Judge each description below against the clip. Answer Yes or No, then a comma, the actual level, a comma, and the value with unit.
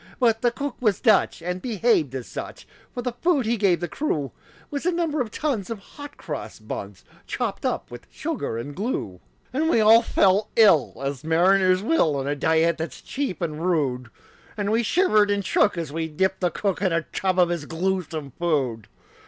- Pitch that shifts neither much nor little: No, wide, 6.6 semitones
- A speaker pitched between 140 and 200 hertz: Yes, medium, 185 Hz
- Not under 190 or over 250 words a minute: Yes, average, 200 wpm